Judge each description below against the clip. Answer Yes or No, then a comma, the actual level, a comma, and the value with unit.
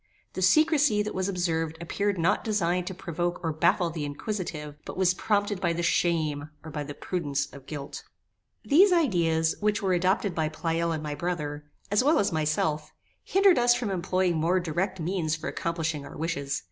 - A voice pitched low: No, medium, 175 Hz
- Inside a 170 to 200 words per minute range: Yes, average, 185 wpm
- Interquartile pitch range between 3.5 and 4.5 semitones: Yes, average, 3.9 semitones